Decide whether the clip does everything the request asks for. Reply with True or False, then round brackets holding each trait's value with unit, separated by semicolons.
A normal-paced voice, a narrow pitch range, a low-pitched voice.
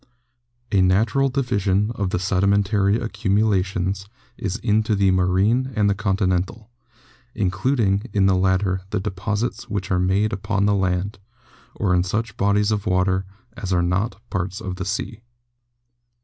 True (150 wpm; 2.2 semitones; 100 Hz)